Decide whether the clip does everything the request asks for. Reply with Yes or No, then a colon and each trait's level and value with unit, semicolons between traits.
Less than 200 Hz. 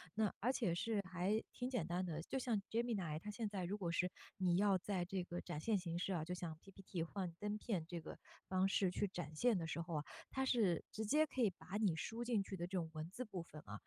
Yes: high, 190 Hz